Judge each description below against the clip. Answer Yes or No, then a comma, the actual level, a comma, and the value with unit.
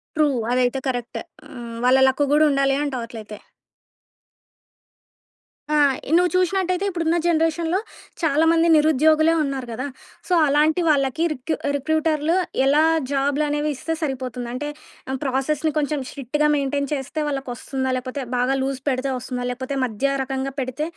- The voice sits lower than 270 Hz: No, very high, 280 Hz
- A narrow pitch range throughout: No, average, 3.2 semitones